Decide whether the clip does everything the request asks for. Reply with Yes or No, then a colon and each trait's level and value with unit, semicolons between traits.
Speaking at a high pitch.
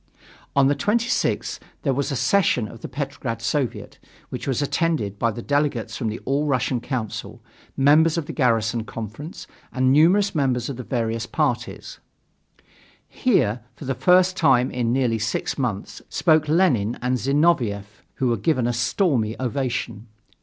No: low, 130 Hz